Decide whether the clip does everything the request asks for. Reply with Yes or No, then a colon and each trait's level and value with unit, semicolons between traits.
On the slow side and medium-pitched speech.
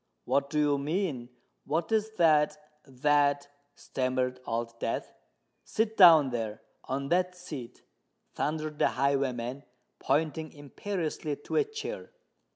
Yes: slow, 100 wpm; medium, 145 Hz